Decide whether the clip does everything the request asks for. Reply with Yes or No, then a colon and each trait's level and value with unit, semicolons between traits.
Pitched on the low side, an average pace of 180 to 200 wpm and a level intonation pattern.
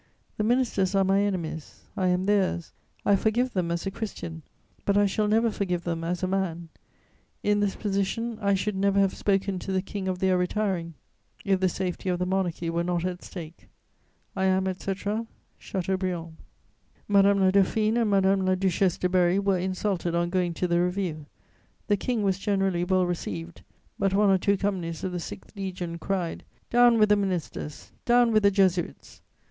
No: high, 190 Hz; average, 185 wpm; narrow, 2.1 semitones